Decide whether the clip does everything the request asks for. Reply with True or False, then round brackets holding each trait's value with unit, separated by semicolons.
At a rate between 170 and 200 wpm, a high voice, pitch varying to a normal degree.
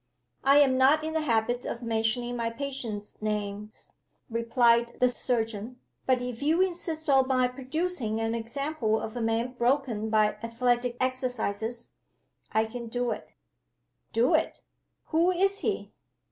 False (145 wpm; 245 Hz; 3.0 semitones)